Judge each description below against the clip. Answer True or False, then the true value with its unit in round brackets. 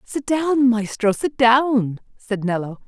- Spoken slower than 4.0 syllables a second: True (3.7 syllables/s)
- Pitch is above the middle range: True (235 Hz)